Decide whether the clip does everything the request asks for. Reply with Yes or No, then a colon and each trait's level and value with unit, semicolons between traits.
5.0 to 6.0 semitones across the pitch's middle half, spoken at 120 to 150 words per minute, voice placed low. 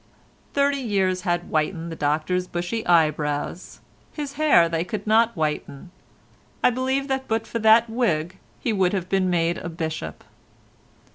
No: wide, 5.6 semitones; average, 145 wpm; medium, 185 Hz